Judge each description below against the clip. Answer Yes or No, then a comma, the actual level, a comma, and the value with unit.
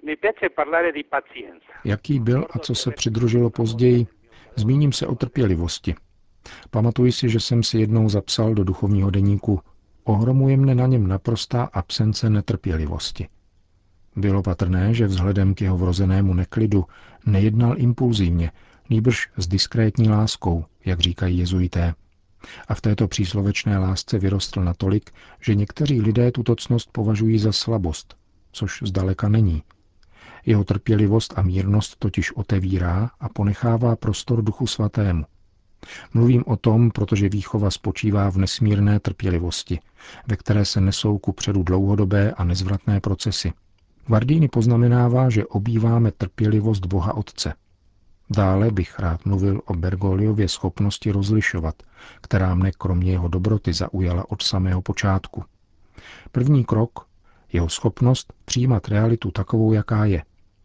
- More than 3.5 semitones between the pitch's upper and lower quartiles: No, average, 3.2 semitones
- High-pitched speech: No, low, 105 Hz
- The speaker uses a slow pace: No, average, 125 wpm